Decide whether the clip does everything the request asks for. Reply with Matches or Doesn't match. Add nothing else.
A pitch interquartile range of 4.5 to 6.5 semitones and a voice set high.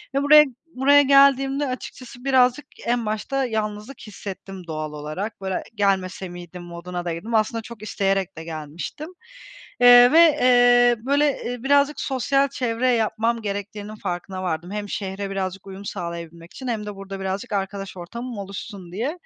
Matches